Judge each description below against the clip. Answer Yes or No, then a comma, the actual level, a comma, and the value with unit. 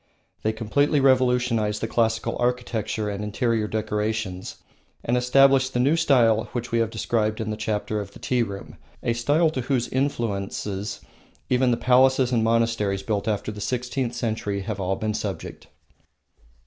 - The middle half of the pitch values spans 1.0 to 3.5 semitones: Yes, average, 2.8 semitones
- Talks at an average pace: Yes, average, 160 wpm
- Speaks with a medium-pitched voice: No, low, 115 Hz